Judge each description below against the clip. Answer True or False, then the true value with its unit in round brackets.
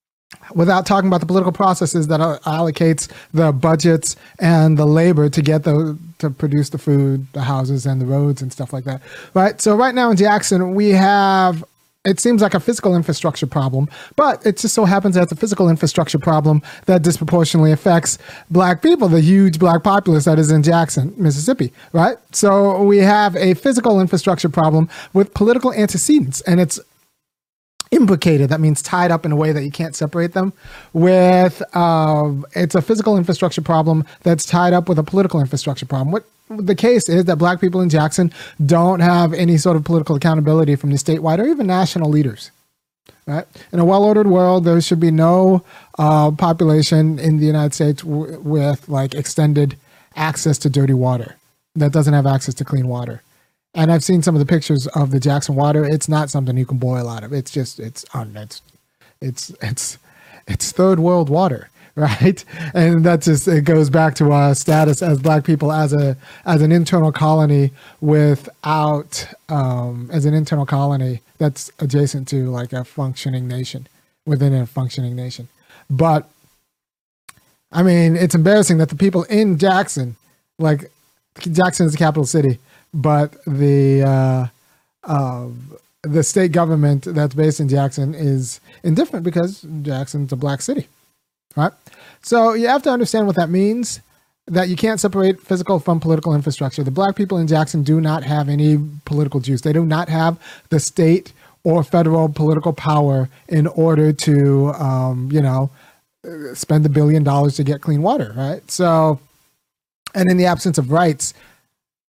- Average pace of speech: True (170 wpm)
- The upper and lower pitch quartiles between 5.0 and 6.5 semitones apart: False (3.7 semitones)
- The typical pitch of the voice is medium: True (155 Hz)